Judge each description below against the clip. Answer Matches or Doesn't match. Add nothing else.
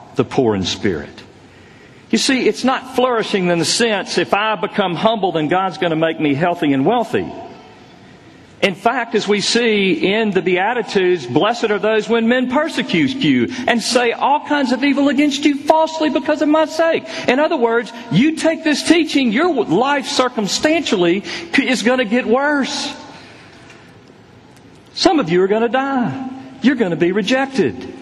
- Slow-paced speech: Doesn't match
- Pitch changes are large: Matches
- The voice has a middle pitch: Doesn't match